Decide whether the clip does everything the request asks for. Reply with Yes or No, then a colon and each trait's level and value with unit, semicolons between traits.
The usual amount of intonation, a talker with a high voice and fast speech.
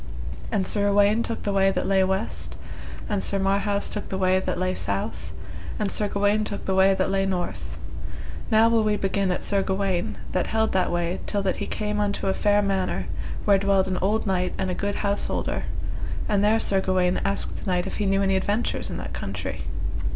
No: narrow, 1.4 semitones; high, 195 Hz; fast, 210 wpm